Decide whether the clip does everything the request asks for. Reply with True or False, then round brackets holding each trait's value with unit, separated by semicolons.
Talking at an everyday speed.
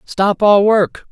True (160 wpm)